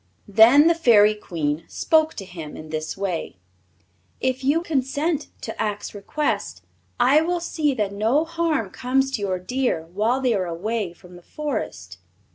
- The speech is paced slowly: No, average, 160 wpm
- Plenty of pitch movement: Yes, wide, 7.7 semitones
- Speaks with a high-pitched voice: Yes, high, 230 Hz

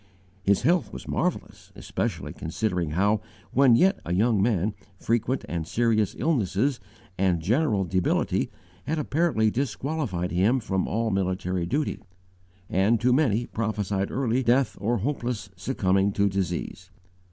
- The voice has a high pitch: No, low, 110 Hz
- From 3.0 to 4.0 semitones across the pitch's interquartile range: No, average, 4.8 semitones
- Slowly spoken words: Yes, slow, 130 wpm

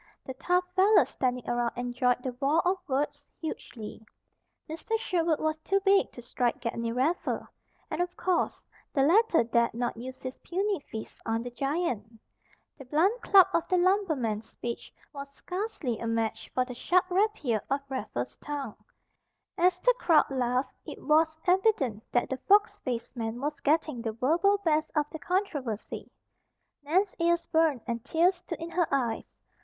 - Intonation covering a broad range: Yes, wide, 6.5 semitones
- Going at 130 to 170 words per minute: Yes, average, 165 wpm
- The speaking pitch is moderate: No, very high, 290 Hz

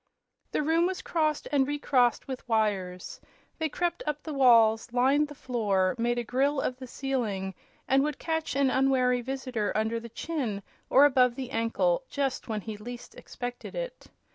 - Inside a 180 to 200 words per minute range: No, average, 170 wpm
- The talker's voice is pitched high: Yes, very high, 255 Hz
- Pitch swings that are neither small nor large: Yes, average, 4.0 semitones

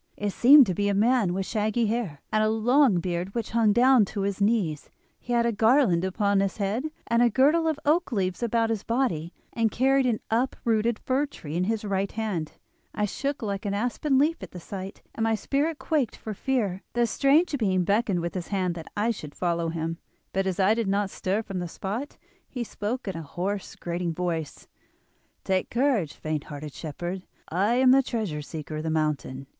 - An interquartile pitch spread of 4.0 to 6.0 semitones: Yes, average, 4.9 semitones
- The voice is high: Yes, high, 205 Hz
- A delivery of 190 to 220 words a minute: Yes, fast, 205 wpm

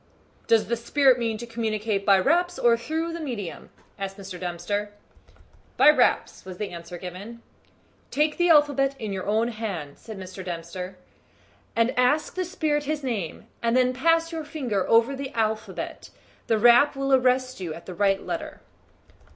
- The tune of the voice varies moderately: No, wide, 6.1 semitones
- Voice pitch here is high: Yes, high, 230 Hz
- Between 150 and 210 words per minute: Yes, average, 165 wpm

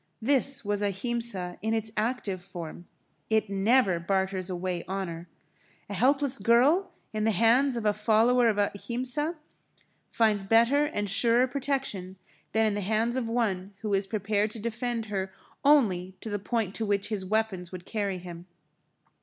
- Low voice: No, high, 215 Hz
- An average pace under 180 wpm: Yes, average, 160 wpm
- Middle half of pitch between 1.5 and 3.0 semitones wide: No, average, 3.7 semitones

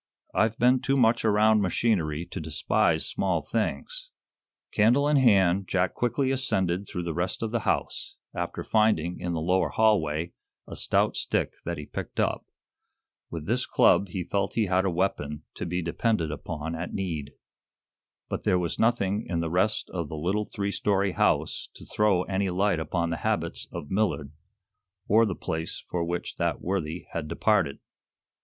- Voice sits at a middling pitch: No, very low, 95 Hz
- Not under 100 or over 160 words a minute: No, average, 170 wpm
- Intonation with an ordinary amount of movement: Yes, average, 4.2 semitones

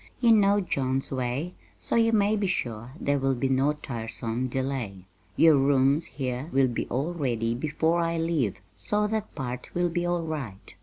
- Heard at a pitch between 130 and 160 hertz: Yes, medium, 140 Hz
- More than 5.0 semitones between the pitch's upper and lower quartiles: Yes, wide, 5.4 semitones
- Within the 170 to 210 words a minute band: Yes, average, 175 wpm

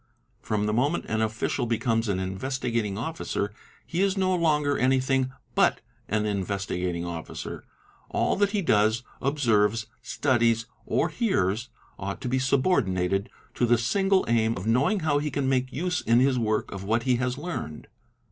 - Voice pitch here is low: Yes, low, 120 Hz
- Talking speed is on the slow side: No, average, 165 wpm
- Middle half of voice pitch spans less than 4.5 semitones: No, average, 5.2 semitones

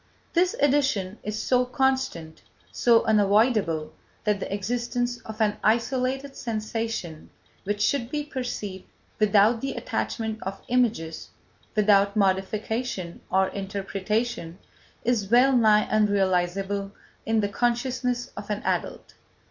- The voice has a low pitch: No, high, 215 Hz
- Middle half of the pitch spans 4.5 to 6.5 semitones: No, average, 3.7 semitones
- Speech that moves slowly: Yes, slow, 115 wpm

